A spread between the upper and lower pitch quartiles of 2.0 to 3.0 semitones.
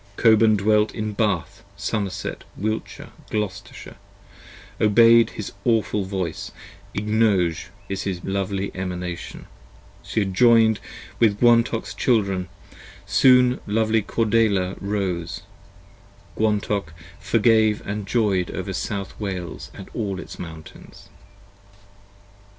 Yes: average, 2.7 semitones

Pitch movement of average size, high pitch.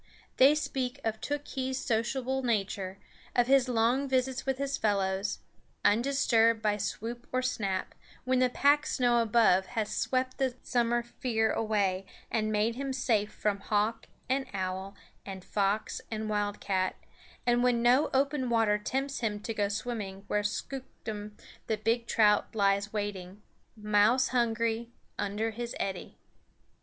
Yes: average, 3.6 semitones; high, 225 Hz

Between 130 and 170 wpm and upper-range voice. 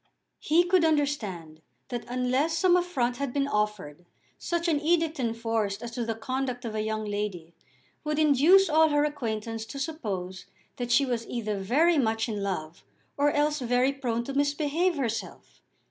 Yes: average, 165 wpm; very high, 250 Hz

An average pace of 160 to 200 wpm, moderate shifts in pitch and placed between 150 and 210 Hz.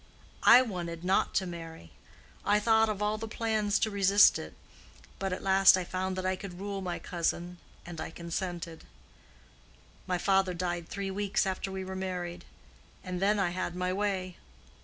No: average, 170 wpm; narrow, 2.2 semitones; medium, 185 Hz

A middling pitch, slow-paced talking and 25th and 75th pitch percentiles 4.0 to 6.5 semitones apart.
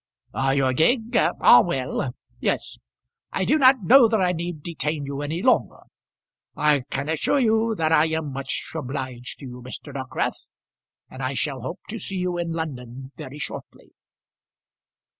No: medium, 155 Hz; average, 160 wpm; average, 5.1 semitones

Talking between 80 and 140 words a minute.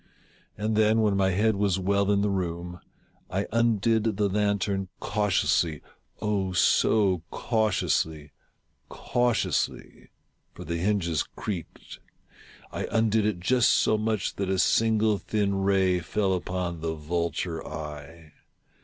Yes: slow, 135 wpm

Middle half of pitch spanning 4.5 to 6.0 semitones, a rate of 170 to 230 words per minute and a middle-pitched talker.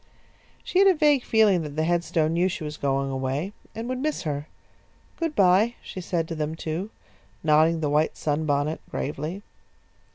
Yes: average, 5.1 semitones; average, 175 wpm; medium, 165 Hz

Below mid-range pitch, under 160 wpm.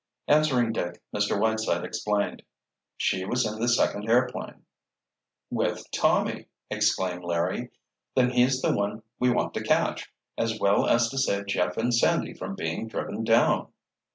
Yes: low, 110 Hz; average, 150 wpm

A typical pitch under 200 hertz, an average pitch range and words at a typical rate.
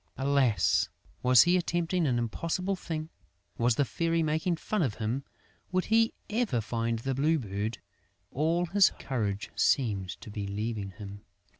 No: low, 135 Hz; wide, 7.1 semitones; average, 150 wpm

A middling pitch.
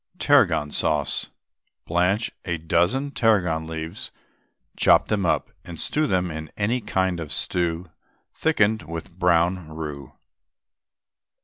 No: very low, 90 Hz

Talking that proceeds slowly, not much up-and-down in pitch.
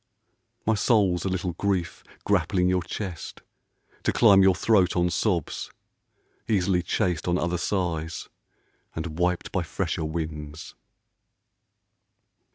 Yes: slow, 115 wpm; narrow, 2.3 semitones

